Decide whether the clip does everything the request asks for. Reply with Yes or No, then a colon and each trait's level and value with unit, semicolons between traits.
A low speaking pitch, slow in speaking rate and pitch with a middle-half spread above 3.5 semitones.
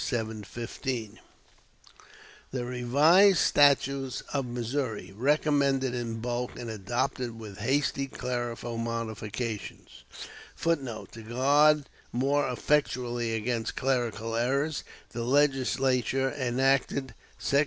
No: low, 125 Hz; slow, 90 wpm; average, 2.9 semitones